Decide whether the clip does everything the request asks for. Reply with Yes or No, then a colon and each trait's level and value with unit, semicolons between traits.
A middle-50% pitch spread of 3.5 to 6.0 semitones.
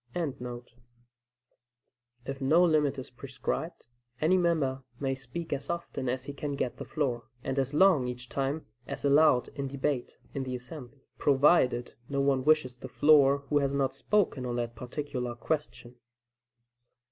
No: average, 3.1 semitones